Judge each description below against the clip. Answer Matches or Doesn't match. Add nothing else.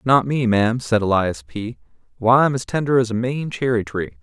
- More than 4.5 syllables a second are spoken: Matches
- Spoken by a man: Matches